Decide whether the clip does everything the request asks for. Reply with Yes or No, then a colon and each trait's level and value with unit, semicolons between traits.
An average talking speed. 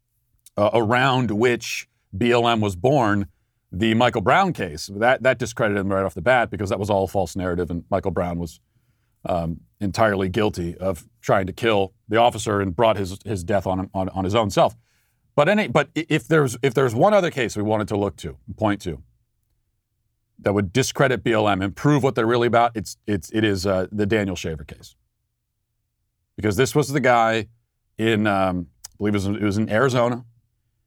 Yes: average, 190 wpm